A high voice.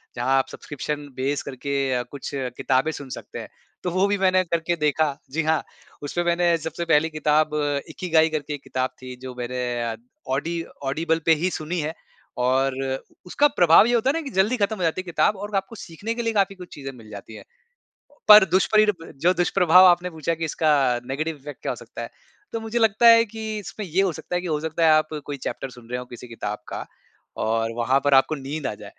No: medium, 160 Hz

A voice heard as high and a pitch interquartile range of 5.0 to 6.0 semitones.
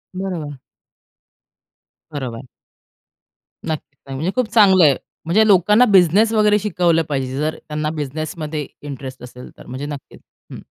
No: medium, 155 Hz; average, 5.3 semitones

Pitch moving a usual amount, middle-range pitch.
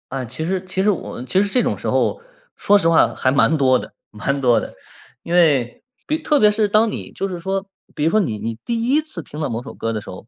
No: wide, 8.1 semitones; medium, 165 Hz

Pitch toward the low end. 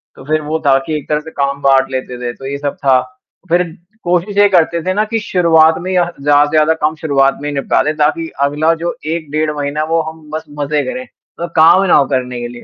No: medium, 155 Hz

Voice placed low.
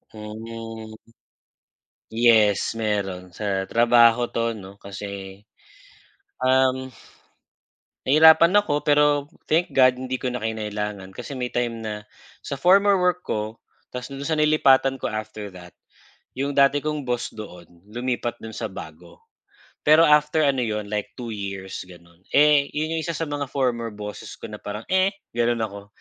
Yes: low, 120 Hz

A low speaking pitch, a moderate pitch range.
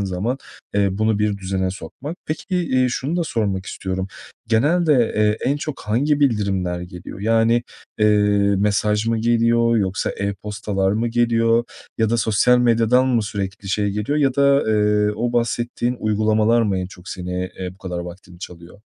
Yes: low, 110 Hz; average, 3.4 semitones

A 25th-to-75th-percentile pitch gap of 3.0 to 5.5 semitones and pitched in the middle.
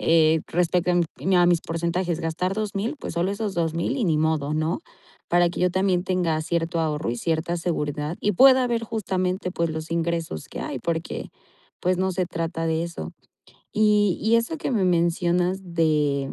No: narrow, 2.5 semitones; medium, 170 Hz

